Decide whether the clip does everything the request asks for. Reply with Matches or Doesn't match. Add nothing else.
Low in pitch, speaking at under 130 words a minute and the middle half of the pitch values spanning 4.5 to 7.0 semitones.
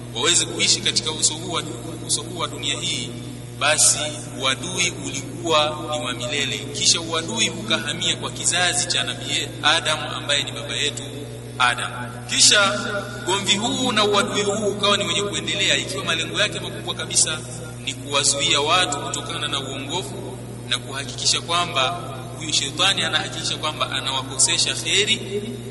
Doesn't match